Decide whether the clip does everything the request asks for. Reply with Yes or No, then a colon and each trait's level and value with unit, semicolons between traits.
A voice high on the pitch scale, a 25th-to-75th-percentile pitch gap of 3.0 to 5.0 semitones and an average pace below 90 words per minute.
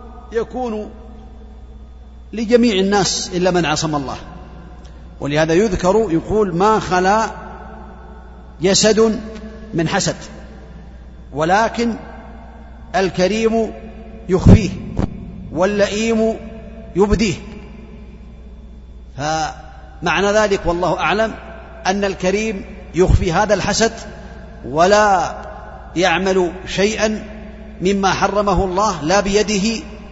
Yes: high, 200 Hz; average, 3.8 semitones; average, 75 wpm